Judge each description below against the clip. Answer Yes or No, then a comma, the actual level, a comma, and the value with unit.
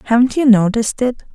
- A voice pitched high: Yes, high, 235 Hz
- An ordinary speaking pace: Yes, average, 180 wpm